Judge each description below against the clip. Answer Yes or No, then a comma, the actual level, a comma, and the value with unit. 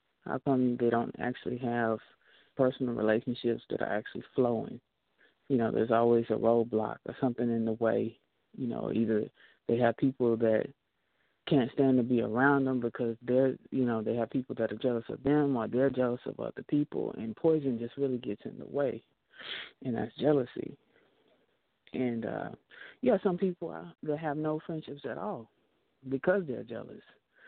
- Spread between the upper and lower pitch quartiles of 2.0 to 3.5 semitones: Yes, average, 3.0 semitones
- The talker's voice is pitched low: Yes, low, 125 Hz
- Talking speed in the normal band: Yes, average, 175 wpm